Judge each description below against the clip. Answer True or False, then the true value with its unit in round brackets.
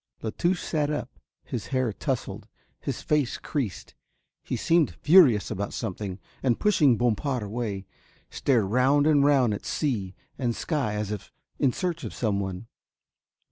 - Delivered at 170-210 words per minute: False (145 wpm)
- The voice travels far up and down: True (5.8 semitones)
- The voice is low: True (125 Hz)